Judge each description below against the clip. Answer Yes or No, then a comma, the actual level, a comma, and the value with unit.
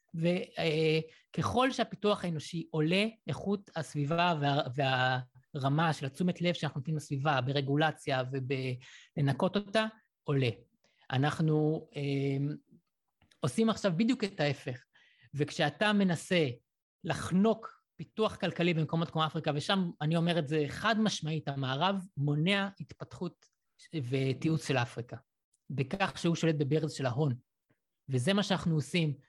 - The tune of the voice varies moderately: Yes, average, 4.2 semitones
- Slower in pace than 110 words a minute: No, average, 115 wpm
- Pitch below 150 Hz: No, medium, 155 Hz